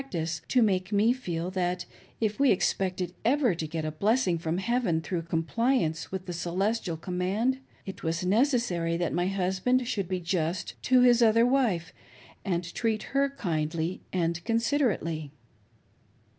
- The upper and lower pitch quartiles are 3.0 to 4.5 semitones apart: No, wide, 5.4 semitones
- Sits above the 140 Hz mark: Yes, medium, 185 Hz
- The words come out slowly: No, average, 155 wpm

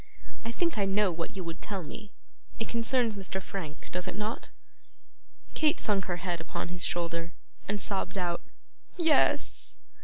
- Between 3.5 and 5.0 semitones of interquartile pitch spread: Yes, average, 3.8 semitones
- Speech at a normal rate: Yes, average, 160 wpm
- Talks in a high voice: Yes, high, 195 Hz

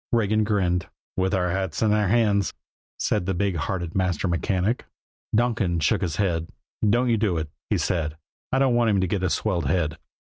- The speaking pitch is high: No, very low, 95 Hz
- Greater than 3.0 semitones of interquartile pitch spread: Yes, average, 3.6 semitones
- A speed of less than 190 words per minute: No, average, 195 wpm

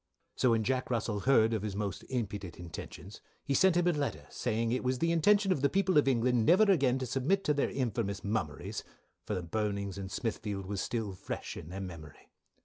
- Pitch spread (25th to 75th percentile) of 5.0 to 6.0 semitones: Yes, wide, 5.4 semitones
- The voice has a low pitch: Yes, low, 115 Hz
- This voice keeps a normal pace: No, fast, 210 wpm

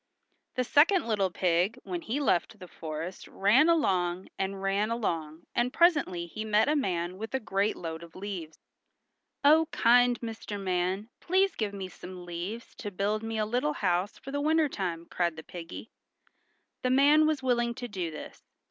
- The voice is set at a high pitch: Yes, high, 210 Hz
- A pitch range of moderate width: No, wide, 5.9 semitones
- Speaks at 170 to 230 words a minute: Yes, average, 175 wpm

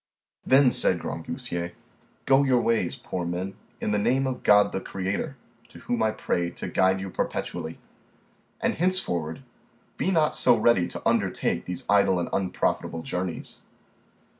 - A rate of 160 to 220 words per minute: No, average, 150 wpm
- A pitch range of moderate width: No, wide, 6.1 semitones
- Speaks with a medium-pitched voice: No, low, 100 Hz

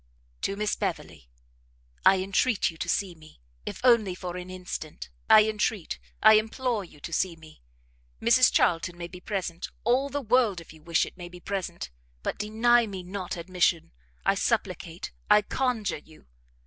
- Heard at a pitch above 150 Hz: Yes, high, 190 Hz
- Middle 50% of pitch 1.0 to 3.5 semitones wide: No, average, 4.2 semitones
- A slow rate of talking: No, average, 170 wpm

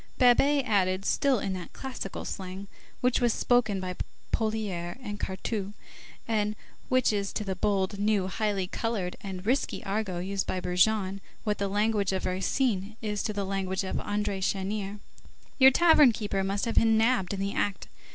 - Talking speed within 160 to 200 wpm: Yes, average, 170 wpm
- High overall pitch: Yes, high, 205 Hz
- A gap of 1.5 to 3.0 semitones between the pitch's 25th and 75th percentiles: Yes, narrow, 2.6 semitones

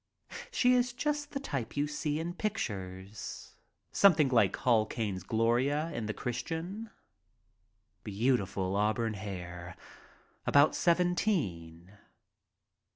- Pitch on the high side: No, low, 120 Hz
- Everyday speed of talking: No, slow, 105 wpm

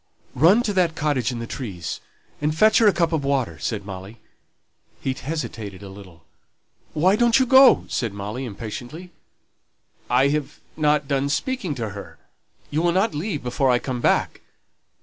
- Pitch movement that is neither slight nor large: No, wide, 6.9 semitones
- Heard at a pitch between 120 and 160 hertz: Yes, medium, 140 Hz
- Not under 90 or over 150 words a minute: No, average, 170 wpm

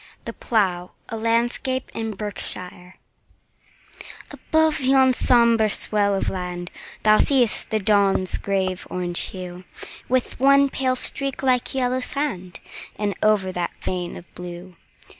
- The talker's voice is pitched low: No, high, 215 Hz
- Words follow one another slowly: Yes, slow, 130 wpm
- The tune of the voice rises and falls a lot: Yes, wide, 5.7 semitones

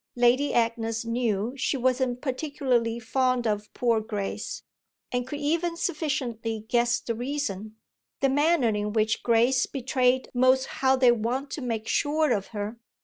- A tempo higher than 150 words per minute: No, average, 145 wpm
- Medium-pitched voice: No, high, 245 Hz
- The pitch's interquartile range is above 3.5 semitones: No, average, 2.8 semitones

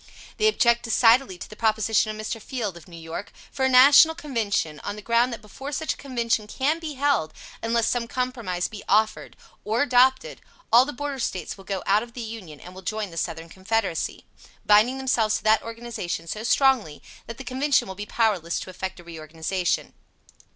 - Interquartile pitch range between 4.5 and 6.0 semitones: Yes, average, 5.0 semitones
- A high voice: Yes, high, 225 Hz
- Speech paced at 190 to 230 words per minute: Yes, average, 195 wpm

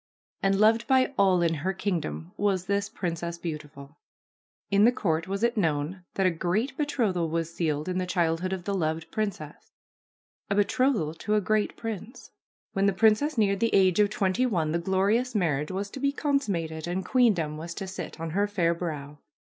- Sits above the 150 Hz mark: Yes, high, 190 Hz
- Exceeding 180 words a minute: Yes, average, 190 wpm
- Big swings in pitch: No, average, 4.3 semitones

